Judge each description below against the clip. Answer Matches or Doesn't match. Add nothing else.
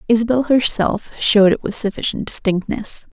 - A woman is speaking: Matches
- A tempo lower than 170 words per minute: Matches